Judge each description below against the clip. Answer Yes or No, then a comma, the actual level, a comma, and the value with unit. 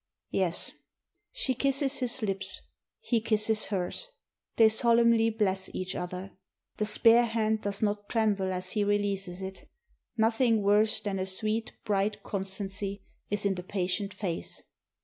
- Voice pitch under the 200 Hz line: No, high, 205 Hz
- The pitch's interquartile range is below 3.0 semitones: Yes, narrow, 2.6 semitones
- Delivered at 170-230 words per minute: No, average, 145 wpm